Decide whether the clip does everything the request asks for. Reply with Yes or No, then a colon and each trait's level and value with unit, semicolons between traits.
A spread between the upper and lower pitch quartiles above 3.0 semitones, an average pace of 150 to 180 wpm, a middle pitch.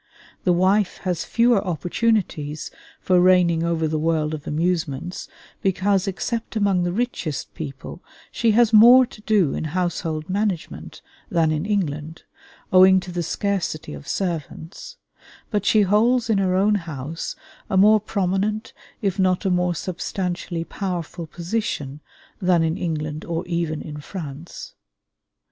No: average, 3.9 semitones; average, 140 wpm; medium, 180 Hz